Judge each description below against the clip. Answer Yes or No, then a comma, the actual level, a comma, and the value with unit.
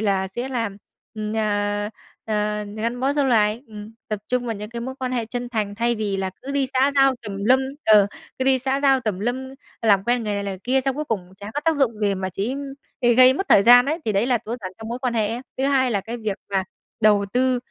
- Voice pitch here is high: Yes, high, 230 Hz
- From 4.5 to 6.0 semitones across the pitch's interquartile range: No, average, 3.7 semitones